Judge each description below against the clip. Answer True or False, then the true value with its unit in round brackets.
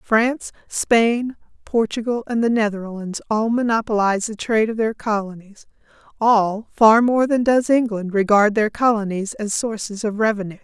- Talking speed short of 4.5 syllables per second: False (4.8 syllables/s)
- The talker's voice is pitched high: True (220 Hz)